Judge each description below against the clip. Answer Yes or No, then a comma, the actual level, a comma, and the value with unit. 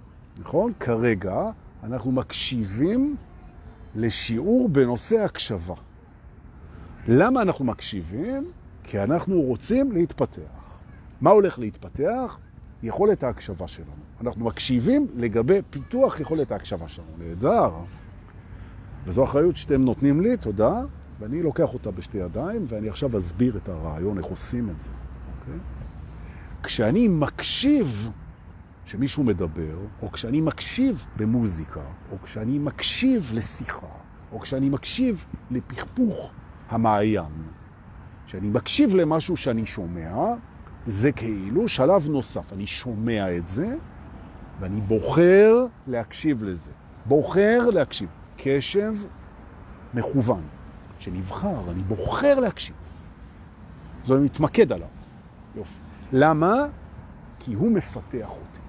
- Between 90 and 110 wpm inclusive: Yes, slow, 100 wpm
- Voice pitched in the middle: No, low, 110 Hz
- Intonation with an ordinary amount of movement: No, wide, 7.9 semitones